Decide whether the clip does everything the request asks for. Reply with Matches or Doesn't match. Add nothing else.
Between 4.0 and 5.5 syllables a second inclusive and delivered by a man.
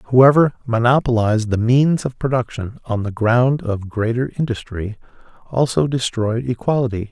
Matches